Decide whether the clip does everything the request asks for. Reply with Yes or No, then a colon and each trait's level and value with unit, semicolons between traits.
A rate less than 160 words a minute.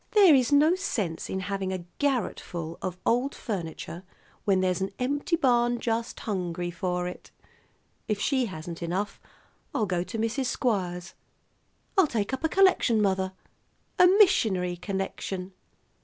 Yes: average, 145 wpm